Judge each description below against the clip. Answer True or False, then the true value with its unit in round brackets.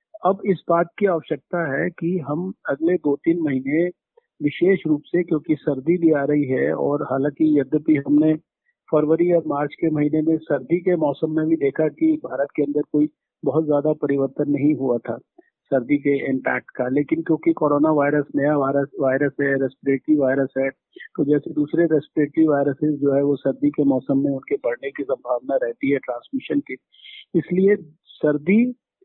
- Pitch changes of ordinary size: True (3.1 semitones)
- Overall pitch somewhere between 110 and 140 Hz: False (150 Hz)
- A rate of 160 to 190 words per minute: True (175 wpm)